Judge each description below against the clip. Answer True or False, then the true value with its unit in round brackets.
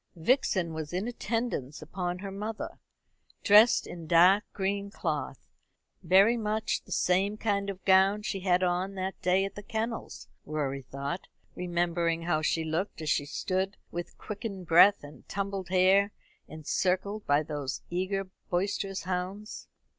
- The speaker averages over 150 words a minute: False (145 wpm)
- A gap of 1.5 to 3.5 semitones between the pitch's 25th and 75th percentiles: True (2.8 semitones)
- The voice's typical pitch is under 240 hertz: True (185 Hz)